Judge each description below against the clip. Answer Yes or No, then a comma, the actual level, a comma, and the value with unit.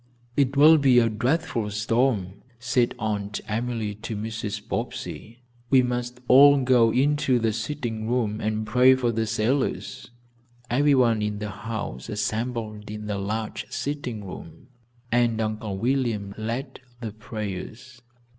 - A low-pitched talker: Yes, low, 115 Hz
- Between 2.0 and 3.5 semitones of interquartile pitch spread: Yes, average, 2.9 semitones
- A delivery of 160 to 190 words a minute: No, slow, 135 wpm